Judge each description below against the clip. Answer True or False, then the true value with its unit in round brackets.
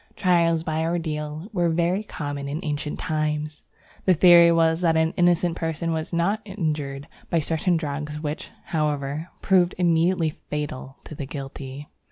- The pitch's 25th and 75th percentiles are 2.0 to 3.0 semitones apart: True (2.4 semitones)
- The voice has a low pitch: False (160 Hz)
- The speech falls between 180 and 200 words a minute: False (150 wpm)